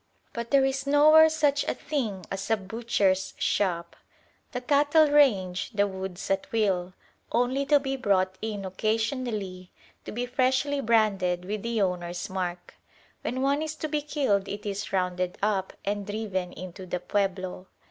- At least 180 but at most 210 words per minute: No, average, 160 wpm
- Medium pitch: No, high, 210 Hz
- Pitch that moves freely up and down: Yes, wide, 6.1 semitones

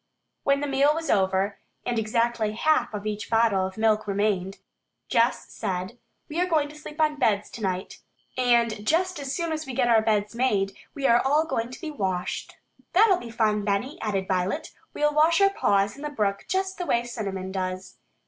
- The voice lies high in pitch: Yes, high, 230 Hz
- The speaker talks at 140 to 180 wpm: No, average, 195 wpm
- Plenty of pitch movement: Yes, wide, 6.6 semitones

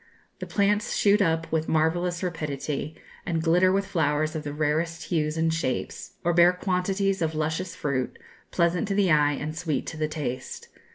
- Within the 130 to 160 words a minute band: No, average, 175 wpm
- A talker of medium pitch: Yes, medium, 165 Hz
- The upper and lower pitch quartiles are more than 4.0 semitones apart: No, average, 2.8 semitones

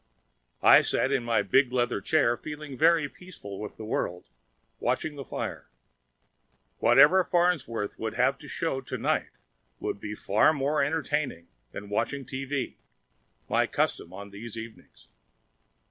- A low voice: Yes, low, 130 Hz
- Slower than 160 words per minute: Yes, average, 140 wpm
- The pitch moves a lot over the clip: Yes, wide, 5.7 semitones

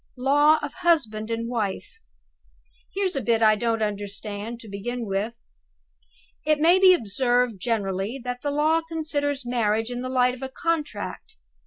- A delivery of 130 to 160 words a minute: Yes, average, 155 wpm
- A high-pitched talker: Yes, high, 245 Hz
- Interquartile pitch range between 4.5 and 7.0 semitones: Yes, average, 5.3 semitones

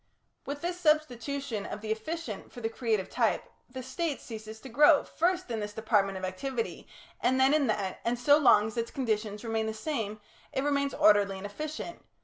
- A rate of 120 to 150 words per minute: No, average, 190 wpm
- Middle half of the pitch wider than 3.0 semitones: Yes, average, 4.9 semitones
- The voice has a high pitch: Yes, high, 235 Hz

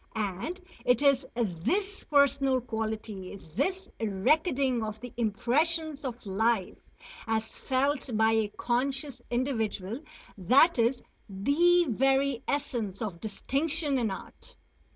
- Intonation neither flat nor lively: Yes, average, 4.4 semitones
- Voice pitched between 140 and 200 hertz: No, high, 245 Hz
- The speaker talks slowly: Yes, slow, 110 wpm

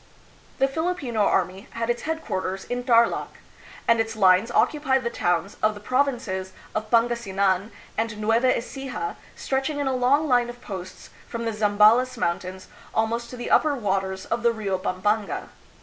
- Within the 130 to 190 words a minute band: Yes, average, 165 wpm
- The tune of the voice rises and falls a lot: No, average, 4.3 semitones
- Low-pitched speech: No, high, 230 Hz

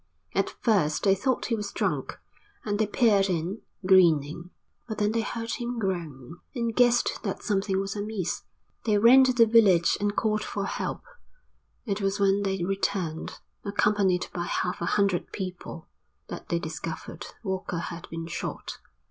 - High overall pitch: Yes, high, 195 Hz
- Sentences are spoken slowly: No, average, 160 wpm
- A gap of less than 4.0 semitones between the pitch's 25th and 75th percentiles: Yes, average, 3.6 semitones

